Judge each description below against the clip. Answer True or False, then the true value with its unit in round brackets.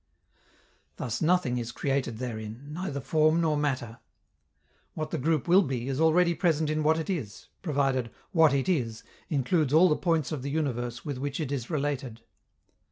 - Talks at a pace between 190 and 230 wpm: False (170 wpm)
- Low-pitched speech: False (145 Hz)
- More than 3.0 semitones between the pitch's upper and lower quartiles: True (4.0 semitones)